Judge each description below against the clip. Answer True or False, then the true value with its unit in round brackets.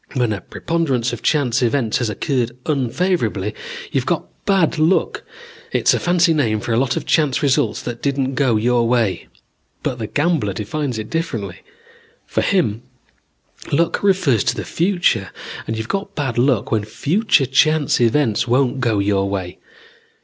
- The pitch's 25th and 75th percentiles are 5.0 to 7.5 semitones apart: True (5.6 semitones)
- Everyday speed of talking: True (160 wpm)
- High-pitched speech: False (130 Hz)